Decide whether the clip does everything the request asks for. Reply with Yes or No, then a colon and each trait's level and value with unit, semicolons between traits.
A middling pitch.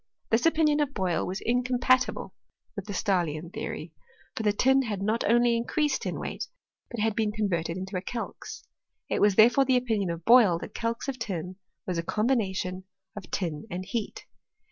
No: high, 215 Hz